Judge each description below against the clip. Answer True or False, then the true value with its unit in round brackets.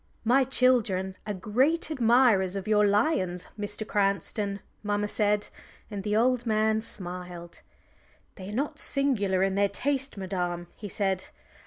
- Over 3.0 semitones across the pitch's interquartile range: True (3.9 semitones)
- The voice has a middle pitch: False (205 Hz)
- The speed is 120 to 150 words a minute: True (140 wpm)